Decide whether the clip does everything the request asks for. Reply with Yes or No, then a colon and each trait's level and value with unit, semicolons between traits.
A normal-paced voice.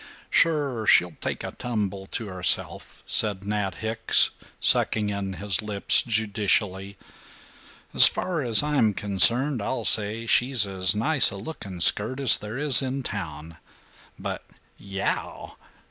No: slow, 130 wpm